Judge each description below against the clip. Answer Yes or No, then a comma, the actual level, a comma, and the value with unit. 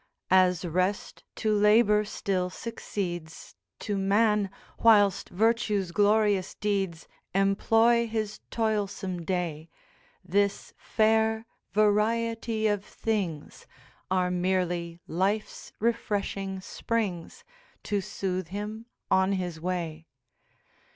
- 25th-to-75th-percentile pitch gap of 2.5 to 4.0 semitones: Yes, average, 3.0 semitones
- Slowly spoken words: Yes, slow, 90 wpm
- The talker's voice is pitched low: No, high, 200 Hz